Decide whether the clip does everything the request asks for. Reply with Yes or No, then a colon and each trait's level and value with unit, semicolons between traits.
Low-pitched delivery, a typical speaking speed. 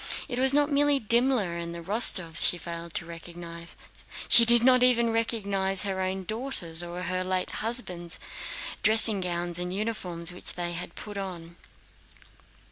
No: medium, 185 Hz; average, 155 wpm